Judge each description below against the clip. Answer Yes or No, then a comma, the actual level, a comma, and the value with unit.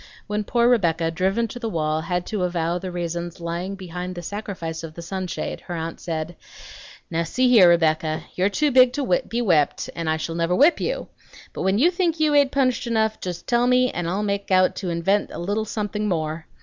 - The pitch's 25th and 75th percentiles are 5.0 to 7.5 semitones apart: Yes, average, 5.3 semitones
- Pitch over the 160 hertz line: Yes, medium, 185 Hz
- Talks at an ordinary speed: No, fast, 215 wpm